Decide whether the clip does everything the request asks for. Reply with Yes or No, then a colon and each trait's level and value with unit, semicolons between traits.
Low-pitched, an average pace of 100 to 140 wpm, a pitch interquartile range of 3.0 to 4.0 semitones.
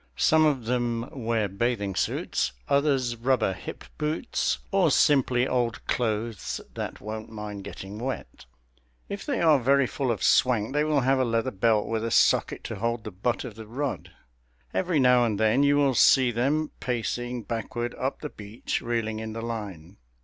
No: low, 120 Hz; average, 175 wpm; average, 3.4 semitones